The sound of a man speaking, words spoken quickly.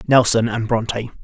No: male; average, 145 wpm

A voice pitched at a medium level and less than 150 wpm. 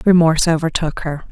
Yes: medium, 165 Hz; slow, 135 wpm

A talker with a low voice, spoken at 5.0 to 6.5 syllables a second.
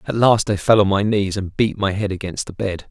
Yes: low, 100 Hz; 5.5 syllables/s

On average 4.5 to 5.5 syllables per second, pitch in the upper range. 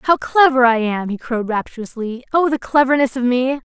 Yes: 5.4 syllables/s; very high, 255 Hz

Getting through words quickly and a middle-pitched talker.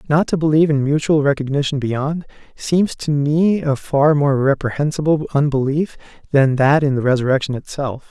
No: average, 155 wpm; medium, 145 Hz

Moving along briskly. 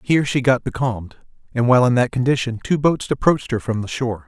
Yes: fast, 225 wpm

